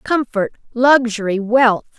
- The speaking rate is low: Yes, slow, 90 wpm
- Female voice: Yes, female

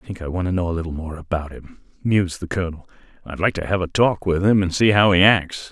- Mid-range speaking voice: No, very low, 90 Hz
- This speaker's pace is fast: Yes, fast, 285 wpm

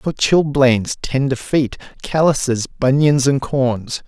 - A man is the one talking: Yes, male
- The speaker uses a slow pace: Yes, slow, 120 wpm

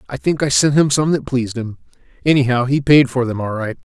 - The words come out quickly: Yes, fast, 245 wpm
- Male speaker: Yes, male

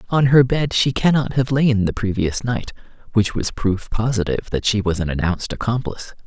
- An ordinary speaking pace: Yes, average, 190 wpm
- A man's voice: Yes, male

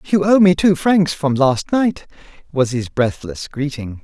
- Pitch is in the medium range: Yes, medium, 155 Hz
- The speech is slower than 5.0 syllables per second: Yes, 4.1 syllables/s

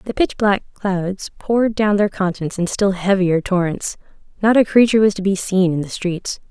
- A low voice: No, high, 195 Hz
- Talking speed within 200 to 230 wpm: Yes, fast, 205 wpm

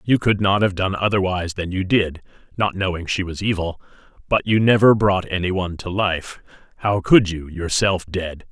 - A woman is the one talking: No, male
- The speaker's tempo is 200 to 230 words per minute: No, average, 185 wpm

